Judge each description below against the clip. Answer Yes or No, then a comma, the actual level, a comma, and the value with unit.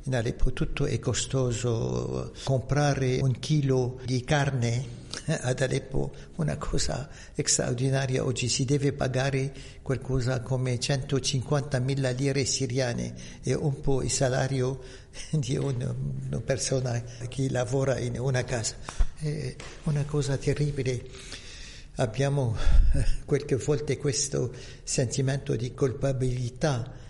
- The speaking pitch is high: No, low, 130 Hz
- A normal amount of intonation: No, narrow, 1.7 semitones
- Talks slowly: Yes, slow, 110 wpm